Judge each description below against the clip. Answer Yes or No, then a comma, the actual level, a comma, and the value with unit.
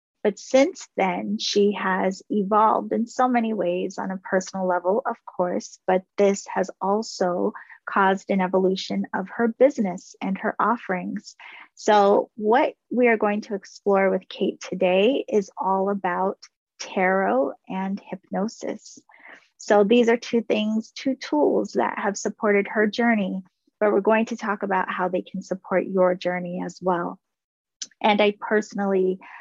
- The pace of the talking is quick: No, average, 150 wpm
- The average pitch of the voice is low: No, high, 200 Hz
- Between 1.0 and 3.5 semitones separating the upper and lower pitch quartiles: Yes, average, 2.8 semitones